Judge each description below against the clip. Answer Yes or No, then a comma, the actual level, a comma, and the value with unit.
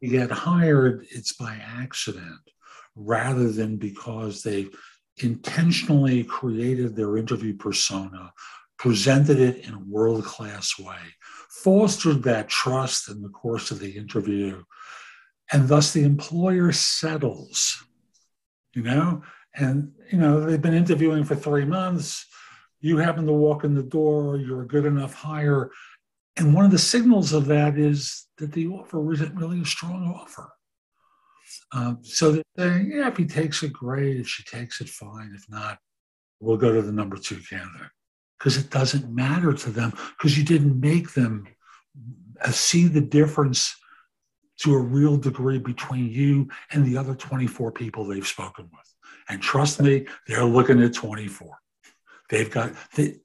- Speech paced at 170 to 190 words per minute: No, average, 155 wpm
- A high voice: No, low, 135 Hz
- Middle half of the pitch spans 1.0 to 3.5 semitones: No, average, 4.9 semitones